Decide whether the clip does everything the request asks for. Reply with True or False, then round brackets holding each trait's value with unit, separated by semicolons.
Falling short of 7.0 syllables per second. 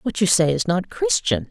True (4.8 syllables/s)